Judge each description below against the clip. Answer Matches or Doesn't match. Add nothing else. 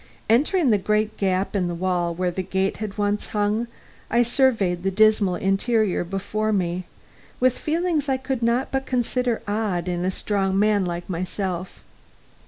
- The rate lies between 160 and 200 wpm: Matches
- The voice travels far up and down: Doesn't match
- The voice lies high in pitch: Matches